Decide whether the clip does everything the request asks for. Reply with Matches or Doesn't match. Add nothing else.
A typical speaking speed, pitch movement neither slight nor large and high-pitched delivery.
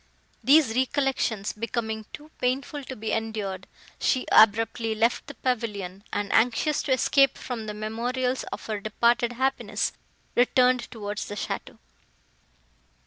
Doesn't match